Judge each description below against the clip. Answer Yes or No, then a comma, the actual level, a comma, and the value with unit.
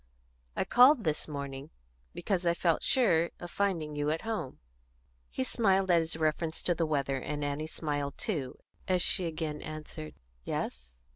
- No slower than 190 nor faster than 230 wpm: No, average, 160 wpm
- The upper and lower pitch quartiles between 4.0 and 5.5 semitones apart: No, average, 3.4 semitones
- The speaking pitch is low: No, medium, 160 Hz